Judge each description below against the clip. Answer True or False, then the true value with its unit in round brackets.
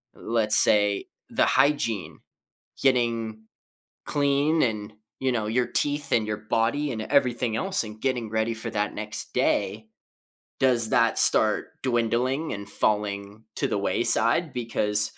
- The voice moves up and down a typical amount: True (3.5 semitones)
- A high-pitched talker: False (115 Hz)